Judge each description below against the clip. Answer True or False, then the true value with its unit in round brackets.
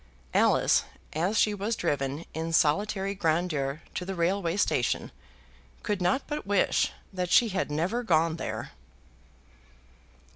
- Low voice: False (180 Hz)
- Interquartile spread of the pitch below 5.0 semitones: True (4.0 semitones)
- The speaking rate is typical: False (125 wpm)